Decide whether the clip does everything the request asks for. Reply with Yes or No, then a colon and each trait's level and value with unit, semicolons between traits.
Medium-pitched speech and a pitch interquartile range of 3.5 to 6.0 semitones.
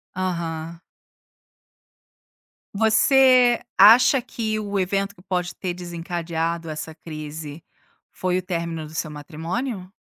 Yes: medium, 180 Hz; average, 3.8 semitones